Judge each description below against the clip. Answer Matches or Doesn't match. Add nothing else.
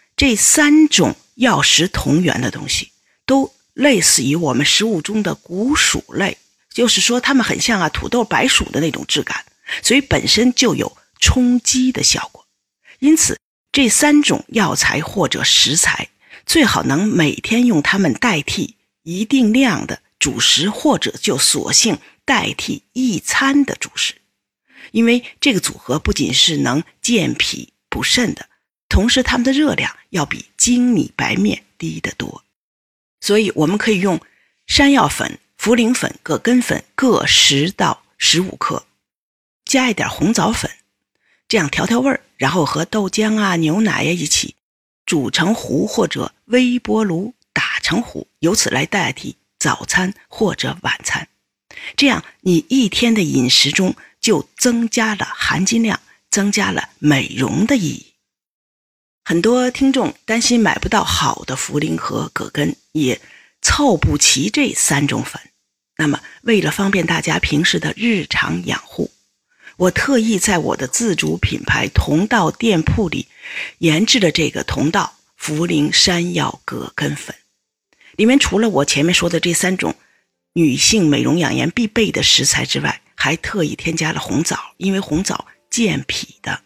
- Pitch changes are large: Matches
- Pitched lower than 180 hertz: Doesn't match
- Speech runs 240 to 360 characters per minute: Doesn't match